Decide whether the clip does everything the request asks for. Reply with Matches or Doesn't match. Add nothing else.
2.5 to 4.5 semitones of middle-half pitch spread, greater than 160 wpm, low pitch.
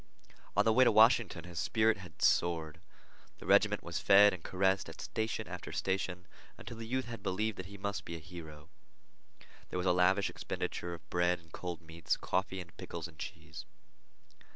Matches